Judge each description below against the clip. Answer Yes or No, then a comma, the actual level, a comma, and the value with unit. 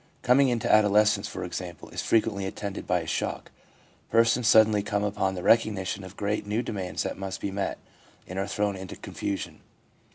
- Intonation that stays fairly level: Yes, narrow, 2.0 semitones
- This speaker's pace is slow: No, average, 175 wpm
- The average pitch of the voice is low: Yes, low, 100 Hz